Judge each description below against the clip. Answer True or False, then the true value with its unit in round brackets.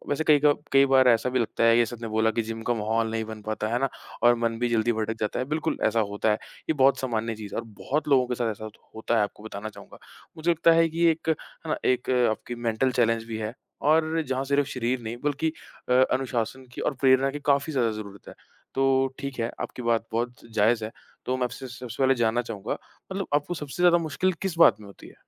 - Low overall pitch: True (120 Hz)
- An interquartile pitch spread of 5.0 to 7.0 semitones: False (3.6 semitones)